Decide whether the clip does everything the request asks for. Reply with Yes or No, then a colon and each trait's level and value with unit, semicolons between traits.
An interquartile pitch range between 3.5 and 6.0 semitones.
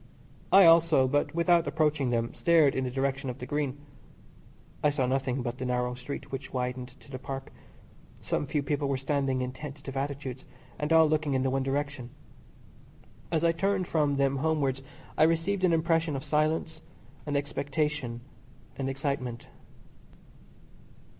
No: average, 2.9 semitones